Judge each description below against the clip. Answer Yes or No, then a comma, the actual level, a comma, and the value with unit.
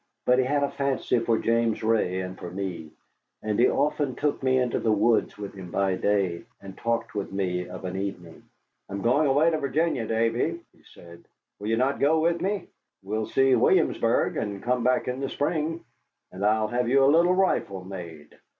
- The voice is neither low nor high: No, low, 115 Hz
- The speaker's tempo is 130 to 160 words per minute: No, average, 195 wpm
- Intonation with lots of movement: Yes, wide, 5.9 semitones